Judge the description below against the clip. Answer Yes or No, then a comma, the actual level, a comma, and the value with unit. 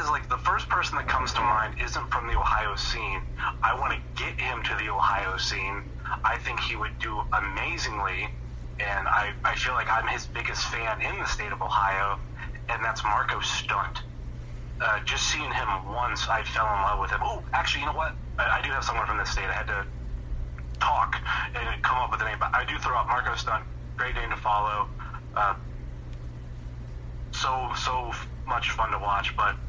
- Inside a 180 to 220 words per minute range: Yes, average, 200 wpm